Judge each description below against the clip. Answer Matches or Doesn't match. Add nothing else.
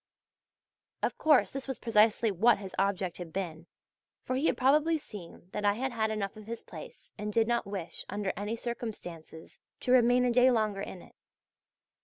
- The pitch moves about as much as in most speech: Matches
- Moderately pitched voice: Doesn't match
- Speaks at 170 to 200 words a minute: Matches